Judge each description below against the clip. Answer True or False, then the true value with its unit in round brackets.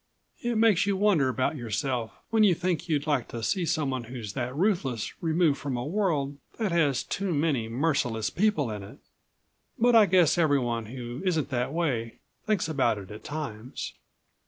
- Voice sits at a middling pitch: True (145 Hz)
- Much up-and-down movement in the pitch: True (6.4 semitones)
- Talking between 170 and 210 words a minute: True (180 wpm)